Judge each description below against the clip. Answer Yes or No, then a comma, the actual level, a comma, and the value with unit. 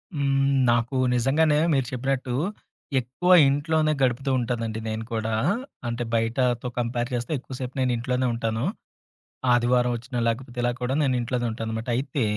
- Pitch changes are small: Yes, narrow, 2.3 semitones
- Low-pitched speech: Yes, low, 125 Hz